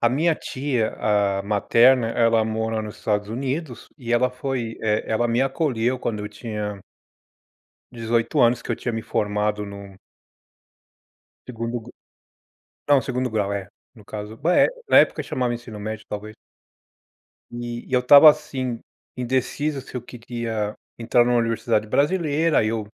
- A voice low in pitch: Yes, low, 115 Hz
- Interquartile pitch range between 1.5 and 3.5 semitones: Yes, average, 2.9 semitones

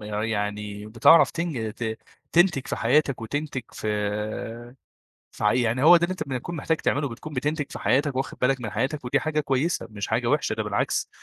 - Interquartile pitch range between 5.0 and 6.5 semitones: Yes, wide, 5.5 semitones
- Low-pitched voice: Yes, low, 125 Hz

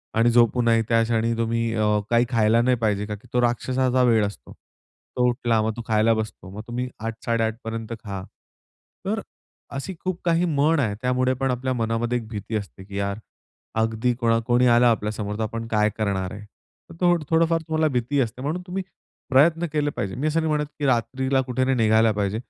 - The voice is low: Yes, low, 120 Hz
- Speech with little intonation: No, average, 3.1 semitones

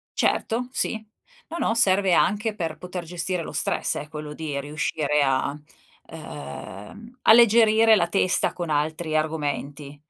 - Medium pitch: Yes, medium, 165 Hz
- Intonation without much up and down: No, wide, 6.2 semitones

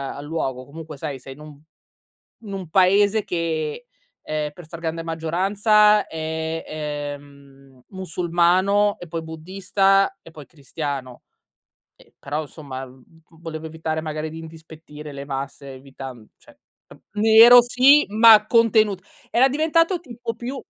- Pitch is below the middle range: No, medium, 160 Hz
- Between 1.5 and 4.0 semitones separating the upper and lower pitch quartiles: No, wide, 5.5 semitones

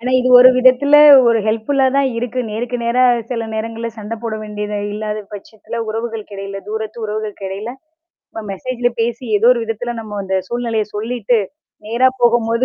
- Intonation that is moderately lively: No, narrow, 2.3 semitones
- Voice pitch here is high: Yes, high, 225 Hz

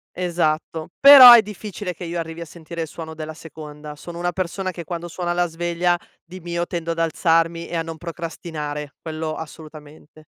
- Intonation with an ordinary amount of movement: No, narrow, 1.7 semitones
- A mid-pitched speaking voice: Yes, medium, 165 Hz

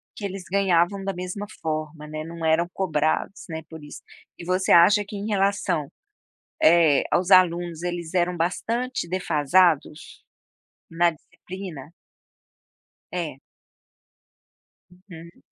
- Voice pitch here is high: No, medium, 175 Hz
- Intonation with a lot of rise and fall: No, average, 2.8 semitones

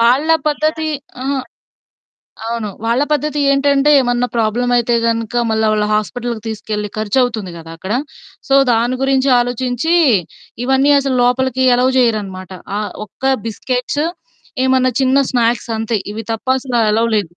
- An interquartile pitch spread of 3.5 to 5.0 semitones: No, average, 3.1 semitones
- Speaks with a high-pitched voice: Yes, high, 245 Hz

